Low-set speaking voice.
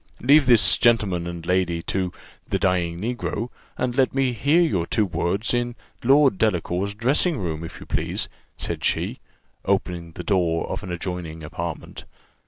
Yes: very low, 95 Hz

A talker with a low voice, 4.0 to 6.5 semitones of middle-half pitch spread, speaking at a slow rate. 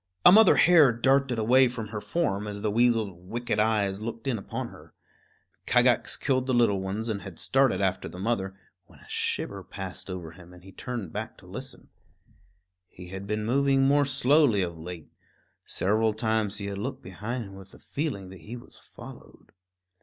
No: low, 110 Hz; average, 4.5 semitones; average, 185 wpm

